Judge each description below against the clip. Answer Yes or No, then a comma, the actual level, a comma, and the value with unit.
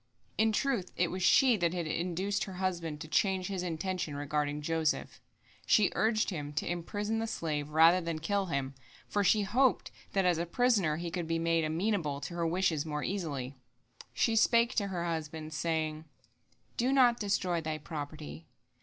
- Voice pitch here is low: No, medium, 170 Hz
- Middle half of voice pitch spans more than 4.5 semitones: No, average, 4.2 semitones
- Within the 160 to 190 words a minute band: Yes, average, 175 wpm